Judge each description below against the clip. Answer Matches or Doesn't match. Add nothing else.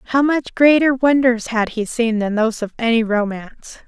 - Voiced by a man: Doesn't match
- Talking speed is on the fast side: Doesn't match